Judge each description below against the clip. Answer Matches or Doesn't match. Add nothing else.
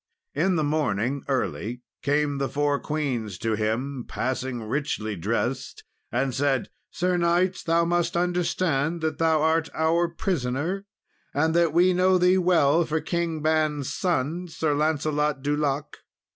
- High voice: Doesn't match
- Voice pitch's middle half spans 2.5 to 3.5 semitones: Doesn't match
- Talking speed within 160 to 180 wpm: Doesn't match